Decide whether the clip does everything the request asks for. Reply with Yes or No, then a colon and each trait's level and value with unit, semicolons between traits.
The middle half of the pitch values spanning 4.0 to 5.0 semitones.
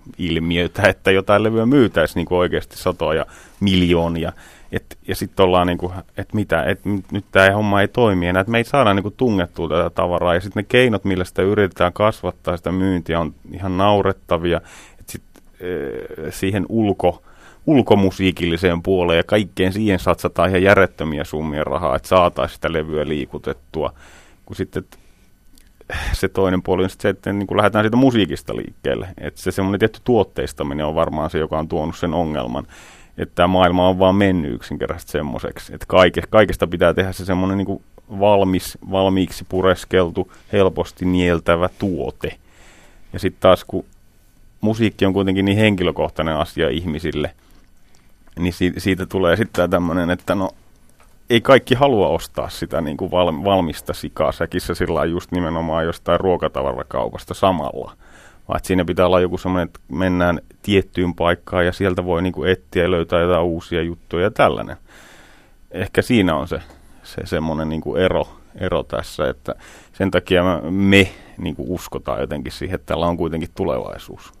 No: narrow, 2.4 semitones